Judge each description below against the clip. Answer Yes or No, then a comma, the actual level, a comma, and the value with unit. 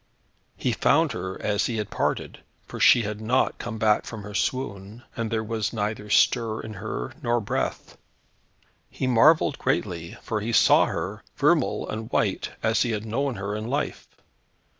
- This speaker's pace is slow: No, average, 170 wpm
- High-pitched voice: No, low, 110 Hz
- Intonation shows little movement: Yes, narrow, 2.2 semitones